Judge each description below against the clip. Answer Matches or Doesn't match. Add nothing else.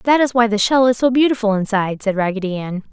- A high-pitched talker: Matches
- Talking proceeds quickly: Matches